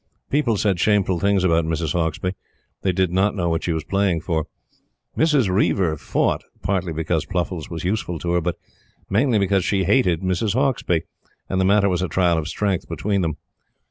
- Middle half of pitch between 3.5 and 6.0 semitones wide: No, average, 3.0 semitones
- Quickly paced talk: No, average, 185 wpm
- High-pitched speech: No, very low, 95 Hz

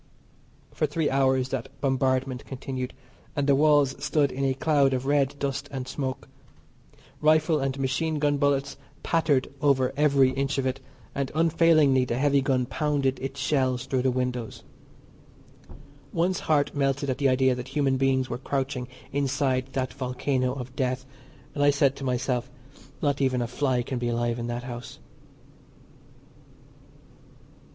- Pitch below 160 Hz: Yes, low, 135 Hz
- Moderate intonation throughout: No, narrow, 1.8 semitones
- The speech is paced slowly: No, average, 155 wpm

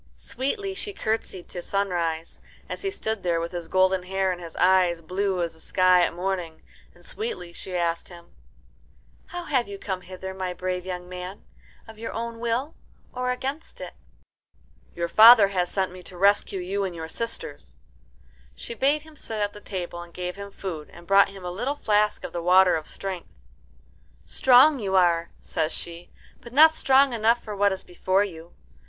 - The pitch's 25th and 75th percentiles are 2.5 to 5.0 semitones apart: Yes, average, 4.2 semitones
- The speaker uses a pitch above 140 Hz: Yes, high, 190 Hz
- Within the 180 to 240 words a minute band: Yes, average, 185 wpm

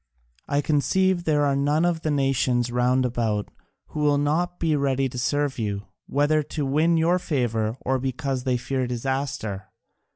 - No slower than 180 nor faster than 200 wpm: No, average, 165 wpm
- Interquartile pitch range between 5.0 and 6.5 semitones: No, average, 3.3 semitones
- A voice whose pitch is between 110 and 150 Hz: Yes, low, 135 Hz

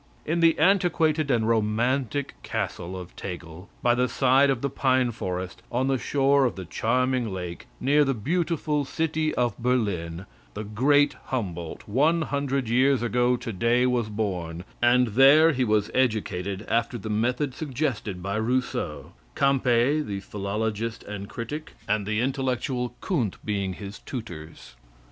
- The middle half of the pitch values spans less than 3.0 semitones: No, average, 4.8 semitones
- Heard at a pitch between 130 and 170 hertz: No, low, 120 Hz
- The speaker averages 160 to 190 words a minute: No, average, 150 wpm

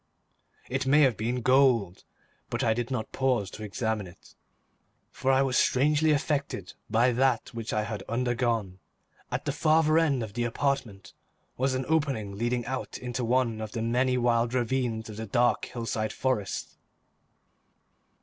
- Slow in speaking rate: No, average, 160 wpm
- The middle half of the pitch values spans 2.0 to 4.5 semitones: Yes, average, 3.1 semitones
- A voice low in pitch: Yes, low, 120 Hz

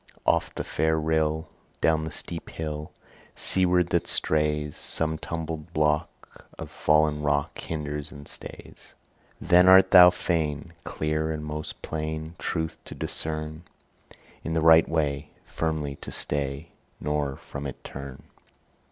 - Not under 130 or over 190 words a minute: Yes, slow, 135 wpm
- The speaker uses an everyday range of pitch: No, narrow, 1.4 semitones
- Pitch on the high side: No, very low, 80 Hz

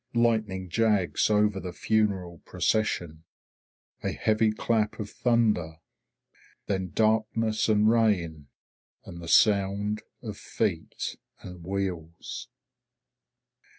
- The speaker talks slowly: Yes, slow, 95 wpm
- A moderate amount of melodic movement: Yes, average, 3.4 semitones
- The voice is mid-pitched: No, low, 105 Hz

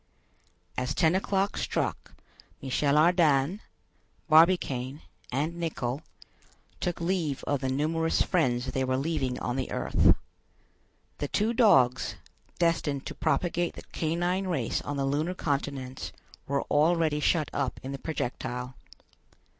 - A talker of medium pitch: Yes, medium, 150 Hz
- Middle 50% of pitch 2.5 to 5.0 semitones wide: Yes, average, 4.2 semitones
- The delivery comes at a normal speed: No, slow, 125 wpm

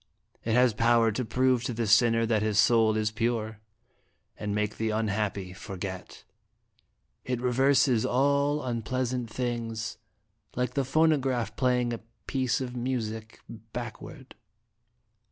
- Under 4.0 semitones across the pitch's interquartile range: Yes, narrow, 2.6 semitones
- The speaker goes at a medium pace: No, slow, 130 wpm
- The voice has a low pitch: Yes, low, 120 Hz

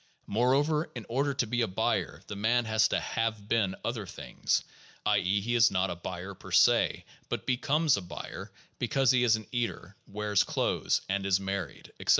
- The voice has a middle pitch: No, low, 110 Hz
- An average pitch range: Yes, average, 3.8 semitones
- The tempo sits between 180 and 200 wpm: Yes, average, 190 wpm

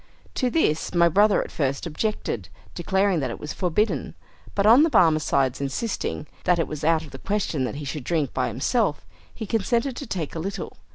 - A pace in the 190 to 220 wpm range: Yes, average, 195 wpm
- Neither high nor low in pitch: Yes, medium, 170 Hz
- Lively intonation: Yes, wide, 6.0 semitones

